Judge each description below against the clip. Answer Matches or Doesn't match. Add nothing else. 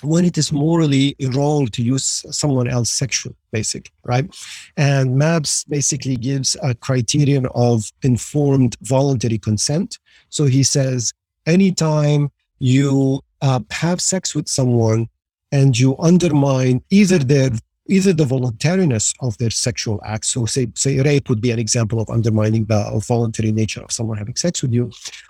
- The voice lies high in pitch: Doesn't match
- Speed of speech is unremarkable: Matches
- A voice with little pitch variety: Doesn't match